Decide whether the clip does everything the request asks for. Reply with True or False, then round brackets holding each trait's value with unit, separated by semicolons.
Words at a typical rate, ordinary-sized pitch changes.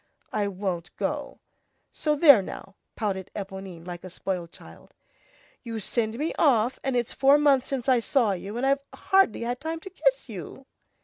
False (175 wpm; 6.2 semitones)